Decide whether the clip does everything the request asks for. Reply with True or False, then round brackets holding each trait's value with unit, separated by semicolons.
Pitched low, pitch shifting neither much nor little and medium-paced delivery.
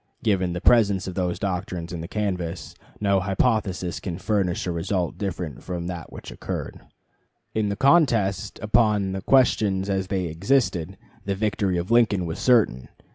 True (95 Hz; 3.0 semitones; 160 wpm)